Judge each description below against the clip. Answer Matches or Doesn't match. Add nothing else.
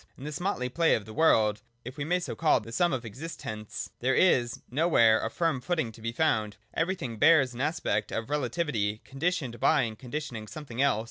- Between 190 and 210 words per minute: Matches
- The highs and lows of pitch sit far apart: Matches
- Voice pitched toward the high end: Doesn't match